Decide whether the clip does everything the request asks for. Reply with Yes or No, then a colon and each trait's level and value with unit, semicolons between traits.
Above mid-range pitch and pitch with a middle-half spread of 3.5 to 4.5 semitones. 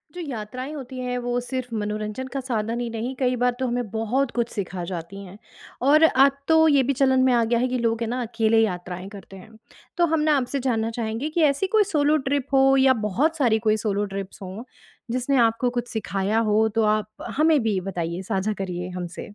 Yes: high, 235 Hz; average, 3.9 semitones